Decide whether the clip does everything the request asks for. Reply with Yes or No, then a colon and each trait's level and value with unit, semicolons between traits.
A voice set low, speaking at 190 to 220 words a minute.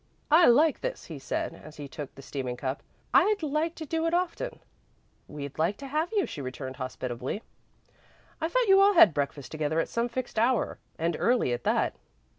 No: high, 215 Hz; average, 195 wpm